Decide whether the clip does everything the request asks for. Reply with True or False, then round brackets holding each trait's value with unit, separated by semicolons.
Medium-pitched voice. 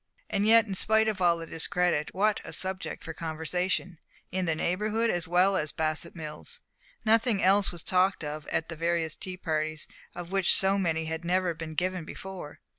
True (180 Hz)